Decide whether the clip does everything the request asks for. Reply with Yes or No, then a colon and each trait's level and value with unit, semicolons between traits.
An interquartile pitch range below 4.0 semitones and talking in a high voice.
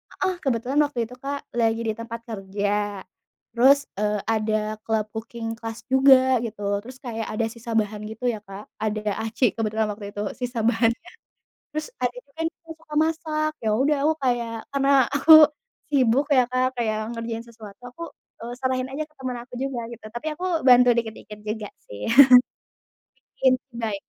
Yes: average, 3.4 semitones; high, 235 Hz